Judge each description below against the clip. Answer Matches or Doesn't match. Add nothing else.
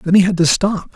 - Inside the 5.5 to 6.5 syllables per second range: Matches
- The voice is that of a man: Matches